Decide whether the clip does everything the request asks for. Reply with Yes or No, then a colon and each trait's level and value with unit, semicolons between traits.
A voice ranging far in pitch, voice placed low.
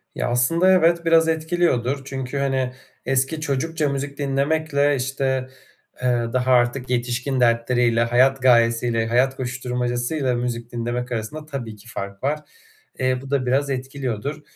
No: narrow, 2.6 semitones; low, 130 Hz